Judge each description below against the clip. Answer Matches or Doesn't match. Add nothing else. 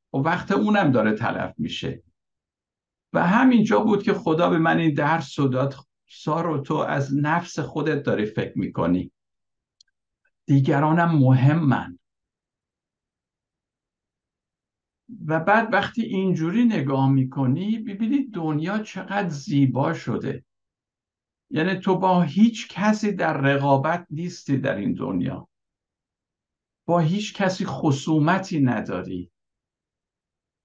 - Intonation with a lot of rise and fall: Matches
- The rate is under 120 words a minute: Matches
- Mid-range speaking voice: Matches